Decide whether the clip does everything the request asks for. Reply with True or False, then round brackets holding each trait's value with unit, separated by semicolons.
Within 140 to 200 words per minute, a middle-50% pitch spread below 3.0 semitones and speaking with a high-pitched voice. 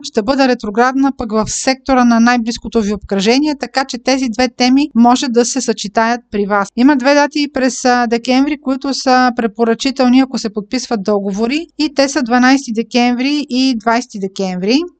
True (165 wpm; 2.5 semitones; 250 Hz)